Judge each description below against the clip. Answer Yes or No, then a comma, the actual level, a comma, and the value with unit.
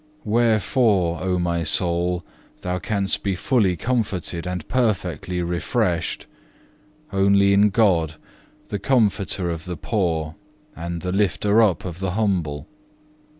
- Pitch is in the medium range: No, very low, 90 Hz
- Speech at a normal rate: No, slow, 120 wpm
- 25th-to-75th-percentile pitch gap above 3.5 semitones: No, average, 3.2 semitones